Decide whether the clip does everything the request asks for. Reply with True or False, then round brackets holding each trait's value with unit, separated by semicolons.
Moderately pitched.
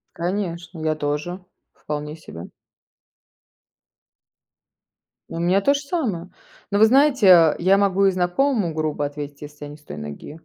True (170 Hz)